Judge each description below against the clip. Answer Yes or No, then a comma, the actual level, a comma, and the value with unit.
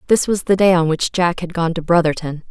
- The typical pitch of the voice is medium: Yes, medium, 175 Hz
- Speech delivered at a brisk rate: Yes, fast, 265 wpm